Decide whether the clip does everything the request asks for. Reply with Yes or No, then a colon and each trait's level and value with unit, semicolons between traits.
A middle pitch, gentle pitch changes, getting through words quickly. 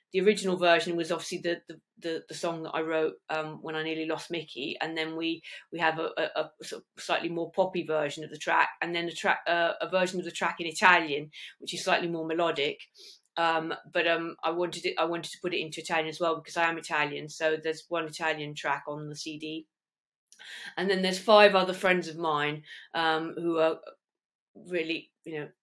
Yes: medium, 165 Hz; narrow, 1.5 semitones; fast, 220 wpm